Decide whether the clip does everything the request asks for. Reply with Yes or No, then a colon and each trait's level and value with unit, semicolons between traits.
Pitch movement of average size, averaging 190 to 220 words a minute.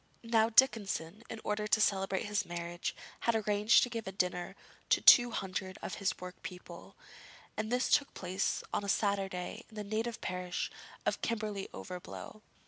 No: average, 3.1 semitones; average, 160 wpm